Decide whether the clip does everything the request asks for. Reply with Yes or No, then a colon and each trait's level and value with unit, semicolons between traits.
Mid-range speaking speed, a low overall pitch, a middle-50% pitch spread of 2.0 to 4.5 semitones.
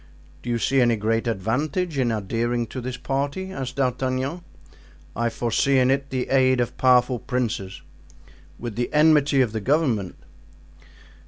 Yes: average, 150 wpm; low, 125 Hz; average, 2.7 semitones